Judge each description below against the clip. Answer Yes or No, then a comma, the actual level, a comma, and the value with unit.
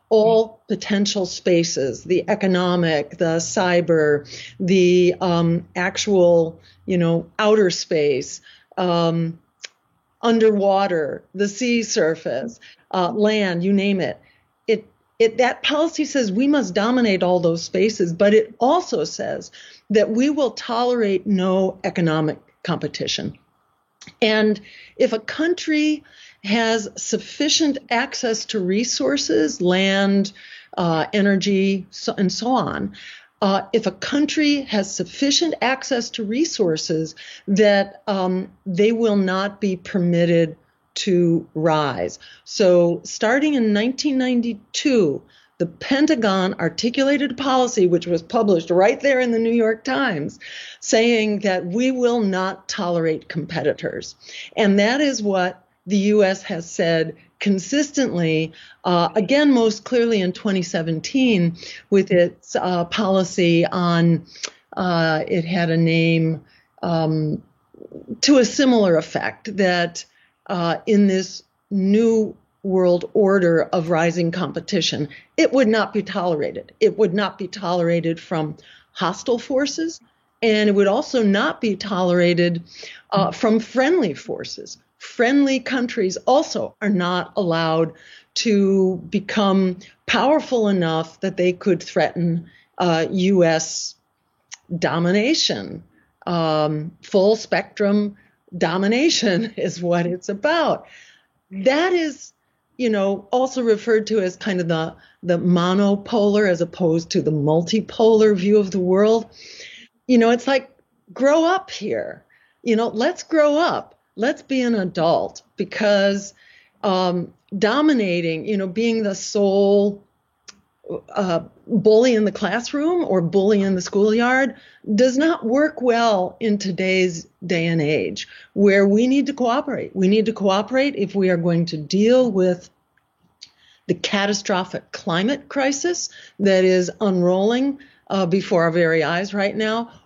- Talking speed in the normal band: No, slow, 125 wpm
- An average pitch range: Yes, average, 4.7 semitones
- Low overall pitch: No, high, 200 Hz